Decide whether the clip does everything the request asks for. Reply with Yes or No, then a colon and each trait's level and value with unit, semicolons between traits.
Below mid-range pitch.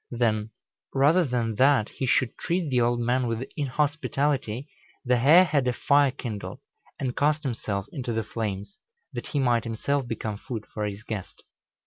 Yes: low, 125 Hz